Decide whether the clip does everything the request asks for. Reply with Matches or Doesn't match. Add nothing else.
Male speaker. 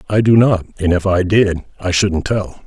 Matches